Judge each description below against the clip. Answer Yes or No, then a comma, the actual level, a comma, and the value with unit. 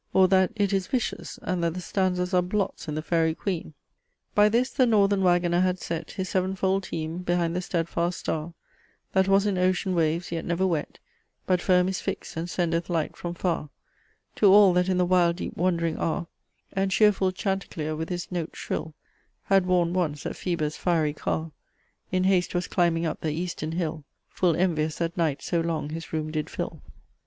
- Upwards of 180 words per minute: Yes, average, 190 wpm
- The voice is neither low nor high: Yes, medium, 175 Hz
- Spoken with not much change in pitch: Yes, narrow, 2.2 semitones